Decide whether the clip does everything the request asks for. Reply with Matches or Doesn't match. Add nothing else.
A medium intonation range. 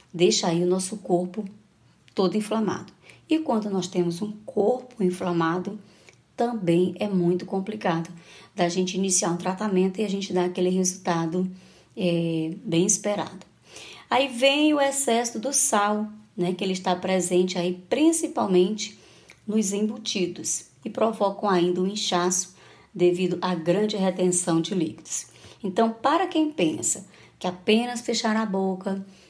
Matches